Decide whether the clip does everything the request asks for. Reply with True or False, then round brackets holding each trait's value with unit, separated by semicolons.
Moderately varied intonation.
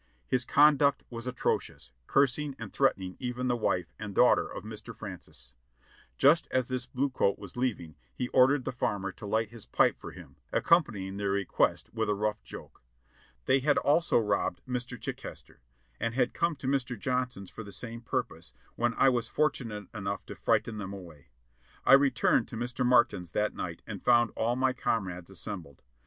True (4.2 semitones)